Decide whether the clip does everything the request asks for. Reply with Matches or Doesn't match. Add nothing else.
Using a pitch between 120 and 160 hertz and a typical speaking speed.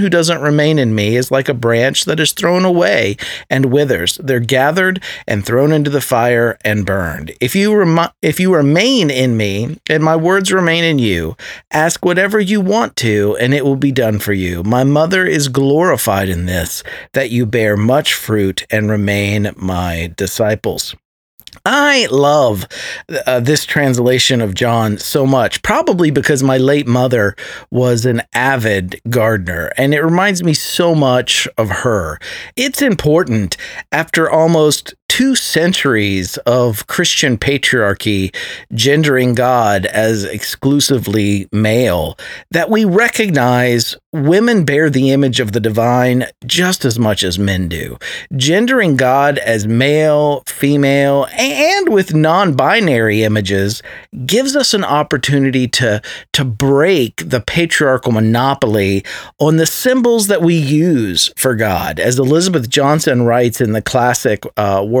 Matches